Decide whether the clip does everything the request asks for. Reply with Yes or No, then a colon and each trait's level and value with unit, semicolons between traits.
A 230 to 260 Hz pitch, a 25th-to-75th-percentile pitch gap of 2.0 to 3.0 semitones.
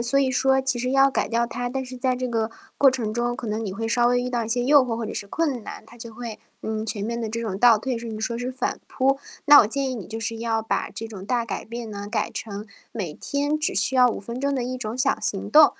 Yes: high, 235 Hz; narrow, 2.5 semitones